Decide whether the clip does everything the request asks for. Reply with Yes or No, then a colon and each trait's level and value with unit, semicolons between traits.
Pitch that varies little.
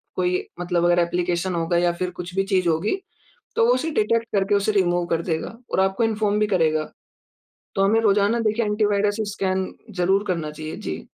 No: average, 3.1 semitones